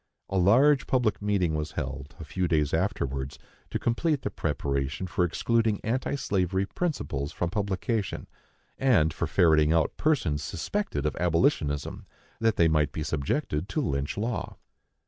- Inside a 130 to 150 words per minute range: Yes, average, 145 wpm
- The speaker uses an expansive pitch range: Yes, wide, 7.0 semitones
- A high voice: No, very low, 90 Hz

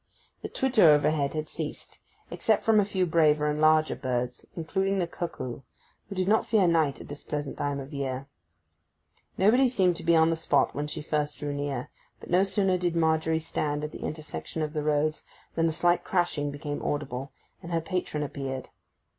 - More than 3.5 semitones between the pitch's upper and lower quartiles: No, average, 3.2 semitones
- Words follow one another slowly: No, average, 190 wpm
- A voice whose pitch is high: No, medium, 155 Hz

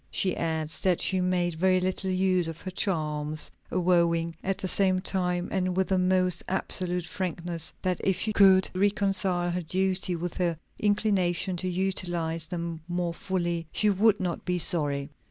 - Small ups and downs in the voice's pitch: Yes, narrow, 1.8 semitones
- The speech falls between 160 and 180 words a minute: Yes, average, 165 wpm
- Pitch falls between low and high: Yes, medium, 180 Hz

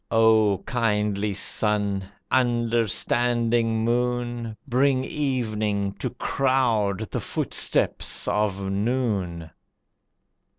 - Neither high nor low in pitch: No, low, 110 Hz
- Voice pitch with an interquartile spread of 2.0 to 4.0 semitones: Yes, average, 2.8 semitones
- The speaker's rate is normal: No, slow, 75 wpm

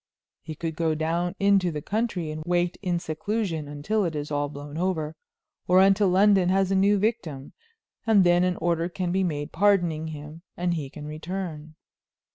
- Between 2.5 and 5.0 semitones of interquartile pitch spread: Yes, average, 3.7 semitones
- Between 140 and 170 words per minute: No, average, 180 wpm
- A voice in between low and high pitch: Yes, medium, 175 Hz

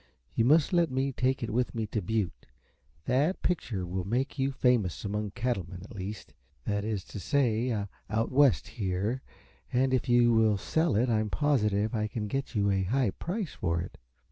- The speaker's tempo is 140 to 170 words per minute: No, average, 190 wpm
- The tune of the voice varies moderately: Yes, average, 4.4 semitones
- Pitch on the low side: Yes, low, 115 Hz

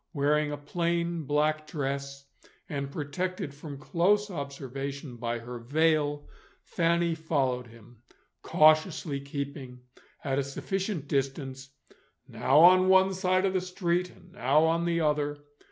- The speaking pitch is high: No, medium, 150 Hz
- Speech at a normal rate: No, slow, 130 wpm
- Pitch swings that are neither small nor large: Yes, average, 3.7 semitones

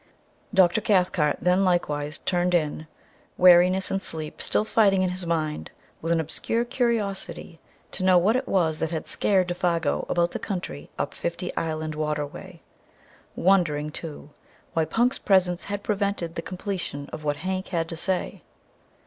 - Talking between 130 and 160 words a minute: Yes, average, 155 wpm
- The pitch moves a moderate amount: Yes, average, 3.2 semitones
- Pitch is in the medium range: Yes, medium, 175 Hz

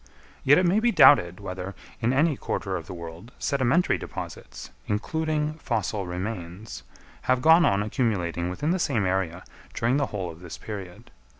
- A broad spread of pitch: Yes, wide, 7.9 semitones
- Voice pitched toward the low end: Yes, low, 105 Hz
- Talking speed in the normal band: Yes, average, 165 wpm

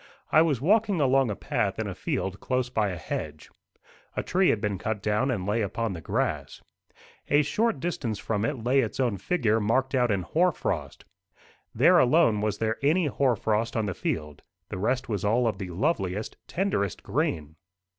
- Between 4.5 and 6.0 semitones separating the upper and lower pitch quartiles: Yes, average, 5.1 semitones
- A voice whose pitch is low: Yes, low, 115 Hz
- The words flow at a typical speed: Yes, average, 190 wpm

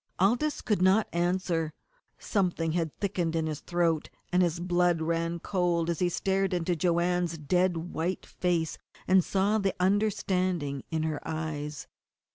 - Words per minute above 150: No, average, 145 wpm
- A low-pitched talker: No, medium, 175 Hz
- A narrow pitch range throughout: Yes, narrow, 2.3 semitones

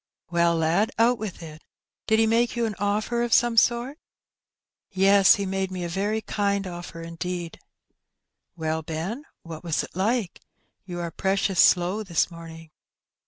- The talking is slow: No, average, 165 wpm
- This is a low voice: No, high, 190 Hz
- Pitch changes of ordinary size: Yes, average, 4.4 semitones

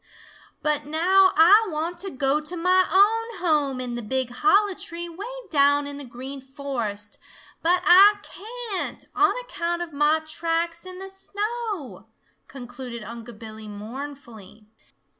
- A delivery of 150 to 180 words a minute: No, average, 140 wpm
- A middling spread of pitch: No, wide, 6.3 semitones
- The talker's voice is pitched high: Yes, very high, 310 Hz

